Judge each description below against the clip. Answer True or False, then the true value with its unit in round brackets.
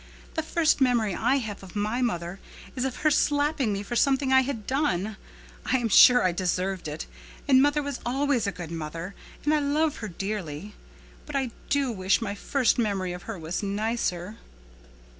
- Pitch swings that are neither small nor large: False (6.2 semitones)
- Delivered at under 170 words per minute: False (185 wpm)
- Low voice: False (225 Hz)